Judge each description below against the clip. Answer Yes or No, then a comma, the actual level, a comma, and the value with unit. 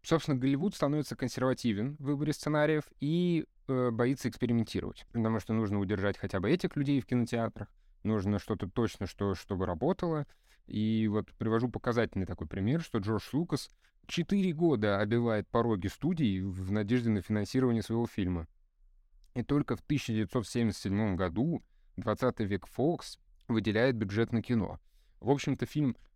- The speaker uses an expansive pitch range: No, average, 4.3 semitones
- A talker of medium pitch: No, low, 115 Hz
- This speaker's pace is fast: No, average, 140 wpm